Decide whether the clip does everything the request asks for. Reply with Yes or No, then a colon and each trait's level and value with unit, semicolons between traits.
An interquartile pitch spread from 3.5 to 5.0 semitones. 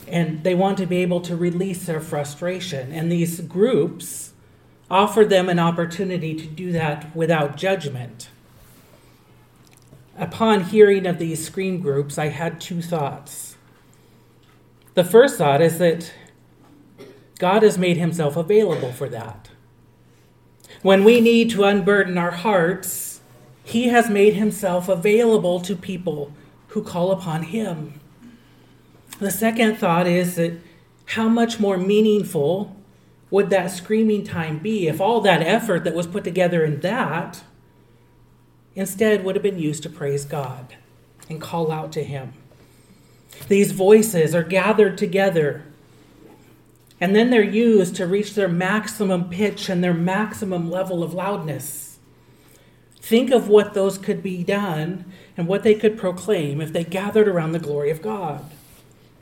Yes: average, 4.3 semitones